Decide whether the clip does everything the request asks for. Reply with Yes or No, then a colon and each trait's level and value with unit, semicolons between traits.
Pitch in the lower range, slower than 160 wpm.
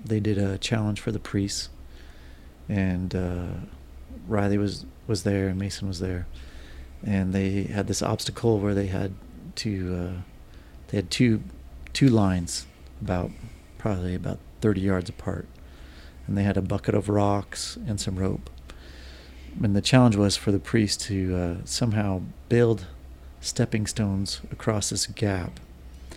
Yes: very low, 95 Hz; average, 145 wpm